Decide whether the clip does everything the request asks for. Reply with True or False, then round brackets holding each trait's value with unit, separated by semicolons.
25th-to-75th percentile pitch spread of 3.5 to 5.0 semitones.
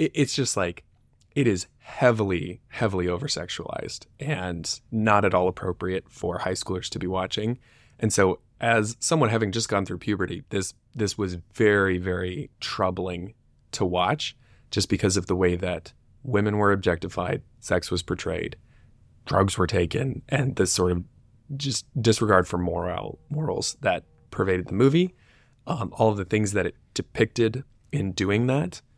True (4.2 semitones)